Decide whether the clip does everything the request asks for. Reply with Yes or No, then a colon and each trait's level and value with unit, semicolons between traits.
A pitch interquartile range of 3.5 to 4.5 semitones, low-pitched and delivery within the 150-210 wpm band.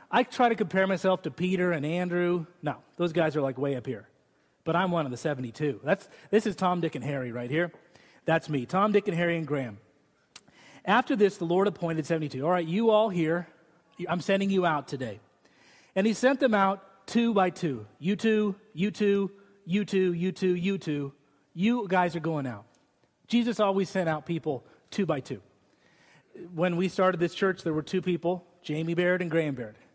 No: average, 4.2 semitones; medium, 175 Hz; average, 200 wpm